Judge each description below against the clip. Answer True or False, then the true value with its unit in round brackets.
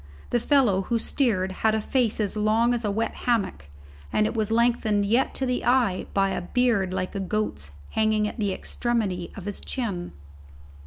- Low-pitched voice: False (215 Hz)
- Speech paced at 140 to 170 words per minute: False (190 wpm)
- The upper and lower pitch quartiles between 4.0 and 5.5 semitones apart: False (3.4 semitones)